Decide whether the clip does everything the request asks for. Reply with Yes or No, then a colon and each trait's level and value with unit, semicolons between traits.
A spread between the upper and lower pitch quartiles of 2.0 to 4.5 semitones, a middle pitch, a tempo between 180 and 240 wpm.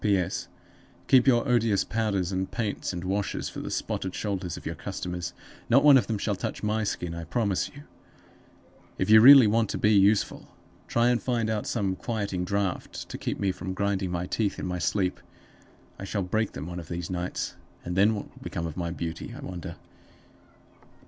No: average, 3.5 semitones; low, 100 Hz; average, 195 wpm